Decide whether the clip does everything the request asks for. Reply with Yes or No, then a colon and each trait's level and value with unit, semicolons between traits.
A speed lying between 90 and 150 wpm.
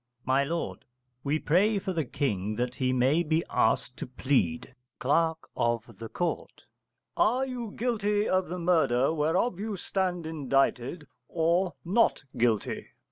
Yes: slow, 135 wpm